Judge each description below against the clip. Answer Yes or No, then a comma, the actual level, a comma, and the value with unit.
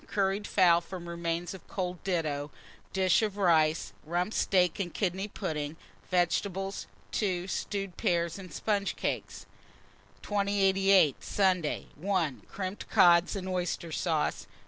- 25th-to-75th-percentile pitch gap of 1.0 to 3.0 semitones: Yes, narrow, 2.5 semitones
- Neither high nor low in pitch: Yes, medium, 180 Hz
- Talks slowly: Yes, slow, 125 wpm